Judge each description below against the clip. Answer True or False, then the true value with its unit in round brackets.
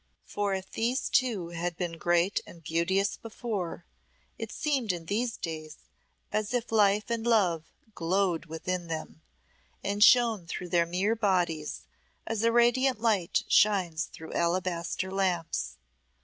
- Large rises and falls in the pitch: False (4.6 semitones)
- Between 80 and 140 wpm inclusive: True (135 wpm)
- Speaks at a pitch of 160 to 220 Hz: True (190 Hz)